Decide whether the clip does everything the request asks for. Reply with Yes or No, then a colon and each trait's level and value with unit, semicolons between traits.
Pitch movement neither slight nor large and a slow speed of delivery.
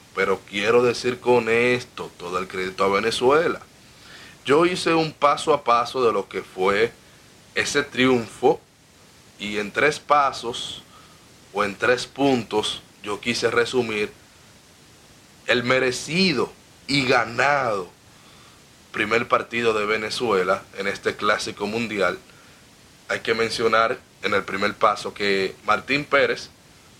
Yes: average, 3.5 semitones; slow, 120 wpm